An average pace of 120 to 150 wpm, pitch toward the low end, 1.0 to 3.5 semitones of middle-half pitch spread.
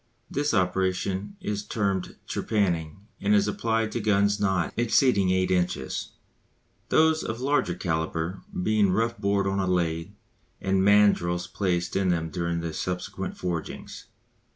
Yes: slow, 135 wpm; very low, 95 Hz; average, 2.9 semitones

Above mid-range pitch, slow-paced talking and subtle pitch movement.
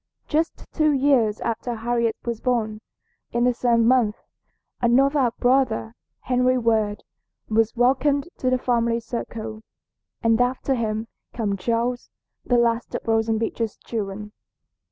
Yes: high, 235 Hz; slow, 130 wpm; narrow, 2.1 semitones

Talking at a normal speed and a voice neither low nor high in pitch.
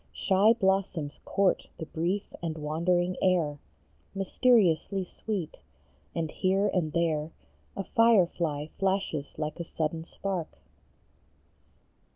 No: slow, 110 wpm; medium, 175 Hz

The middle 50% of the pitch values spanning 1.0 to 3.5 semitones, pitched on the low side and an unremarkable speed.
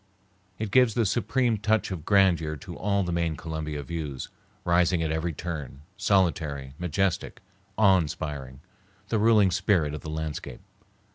No: average, 4.3 semitones; very low, 85 Hz; average, 145 wpm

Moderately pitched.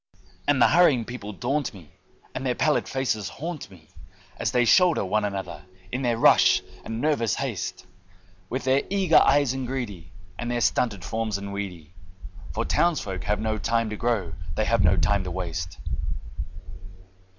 No: low, 115 Hz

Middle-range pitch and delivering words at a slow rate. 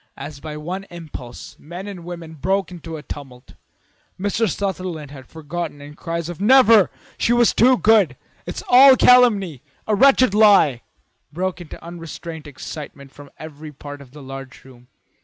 No: medium, 165 Hz; average, 160 wpm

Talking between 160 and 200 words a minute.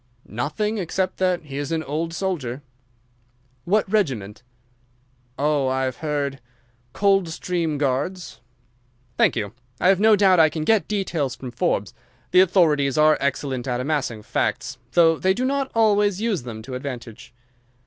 No: average, 145 wpm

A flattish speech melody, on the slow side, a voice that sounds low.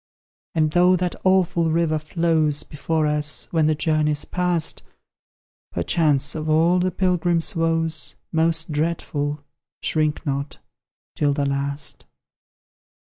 No: narrow, 2.2 semitones; slow, 115 wpm; medium, 155 Hz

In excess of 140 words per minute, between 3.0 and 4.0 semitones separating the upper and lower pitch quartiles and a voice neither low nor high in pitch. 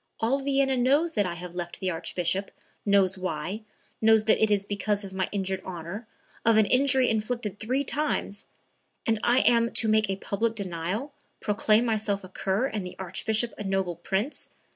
No: average, 180 wpm; average, 3.5 semitones; high, 210 Hz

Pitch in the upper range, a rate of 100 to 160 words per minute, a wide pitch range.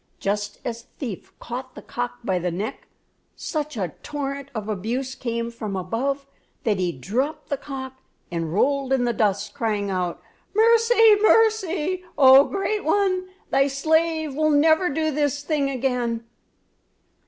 Yes: very high, 270 Hz; average, 150 wpm; wide, 5.8 semitones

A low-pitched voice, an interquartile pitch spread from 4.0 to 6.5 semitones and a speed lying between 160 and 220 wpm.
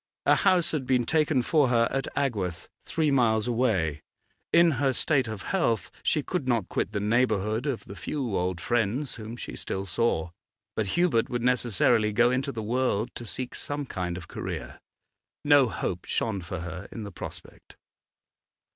Yes: low, 120 Hz; average, 4.6 semitones; average, 175 wpm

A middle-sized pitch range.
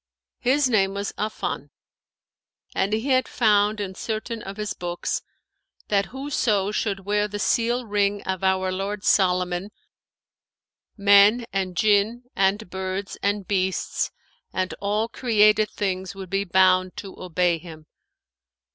No: narrow, 2.1 semitones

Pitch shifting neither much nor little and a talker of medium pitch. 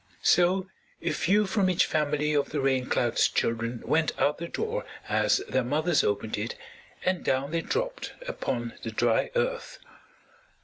No: wide, 7.2 semitones; medium, 150 Hz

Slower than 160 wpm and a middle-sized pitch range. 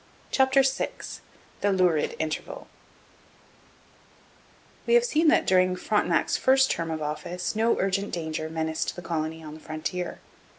No: slow, 135 wpm; wide, 5.7 semitones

